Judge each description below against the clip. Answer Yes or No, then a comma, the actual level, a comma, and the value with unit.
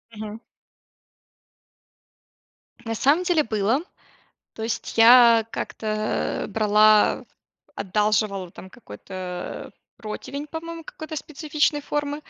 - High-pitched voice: Yes, high, 225 Hz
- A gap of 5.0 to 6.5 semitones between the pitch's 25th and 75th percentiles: Yes, wide, 5.6 semitones